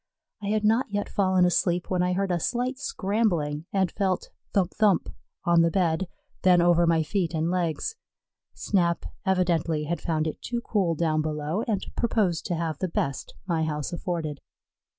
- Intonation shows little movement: No, average, 3.4 semitones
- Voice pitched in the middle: Yes, medium, 175 Hz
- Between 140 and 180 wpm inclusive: Yes, average, 170 wpm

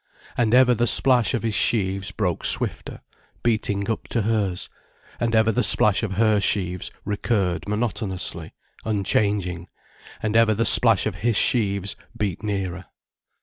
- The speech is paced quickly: No, average, 145 wpm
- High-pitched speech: No, low, 105 Hz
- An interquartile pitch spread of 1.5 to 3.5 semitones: Yes, average, 2.8 semitones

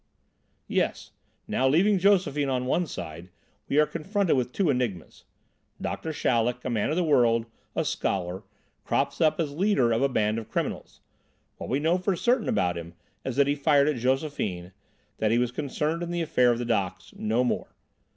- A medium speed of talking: Yes, average, 185 wpm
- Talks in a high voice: No, low, 135 Hz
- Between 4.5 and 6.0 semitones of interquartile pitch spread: Yes, wide, 5.6 semitones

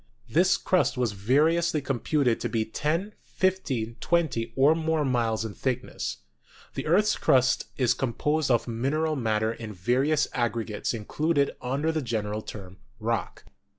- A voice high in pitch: No, low, 130 Hz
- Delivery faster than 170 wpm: No, average, 145 wpm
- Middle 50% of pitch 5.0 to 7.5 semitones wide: Yes, wide, 5.4 semitones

